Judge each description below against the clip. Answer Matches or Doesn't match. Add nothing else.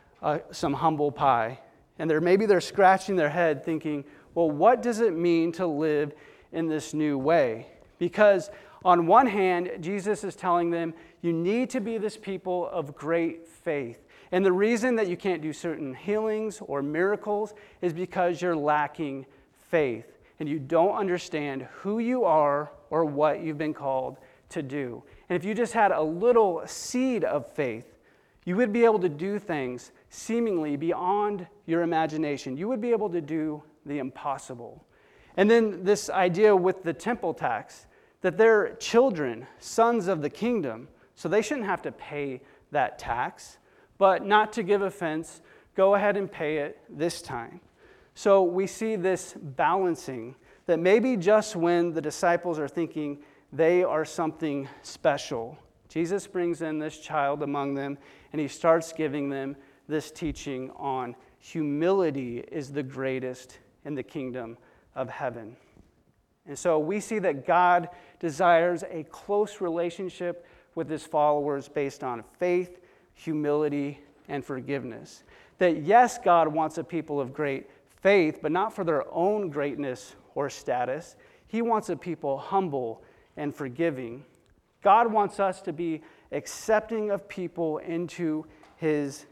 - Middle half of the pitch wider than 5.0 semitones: Doesn't match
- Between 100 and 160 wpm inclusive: Matches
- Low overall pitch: Doesn't match